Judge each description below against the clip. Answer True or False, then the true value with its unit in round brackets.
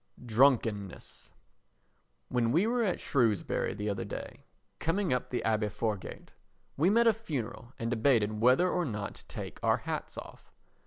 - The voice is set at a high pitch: False (125 Hz)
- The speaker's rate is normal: True (155 wpm)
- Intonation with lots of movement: True (7.6 semitones)